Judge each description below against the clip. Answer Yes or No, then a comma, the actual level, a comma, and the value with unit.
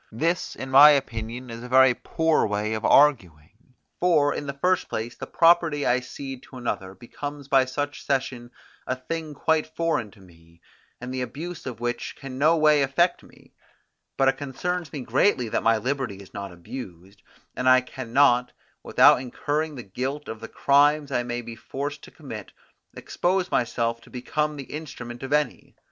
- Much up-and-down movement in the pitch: No, average, 3.8 semitones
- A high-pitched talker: No, low, 130 Hz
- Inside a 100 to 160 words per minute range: No, average, 180 wpm